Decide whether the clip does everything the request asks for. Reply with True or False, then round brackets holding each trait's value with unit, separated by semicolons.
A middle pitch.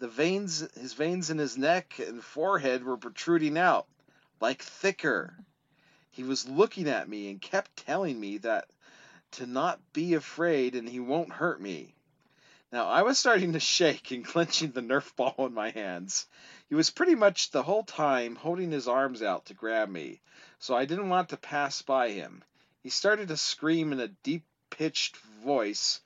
True (150 Hz)